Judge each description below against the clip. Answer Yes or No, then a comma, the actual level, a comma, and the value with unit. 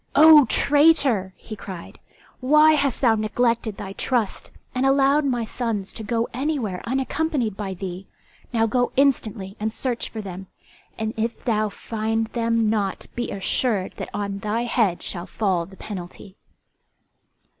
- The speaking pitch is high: Yes, high, 225 Hz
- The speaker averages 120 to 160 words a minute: Yes, average, 145 wpm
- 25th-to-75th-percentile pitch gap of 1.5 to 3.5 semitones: No, average, 4.2 semitones